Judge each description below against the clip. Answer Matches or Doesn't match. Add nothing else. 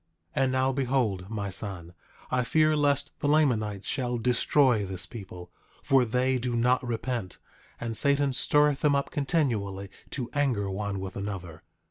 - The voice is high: Doesn't match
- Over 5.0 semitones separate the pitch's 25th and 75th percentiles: Matches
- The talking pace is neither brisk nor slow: Matches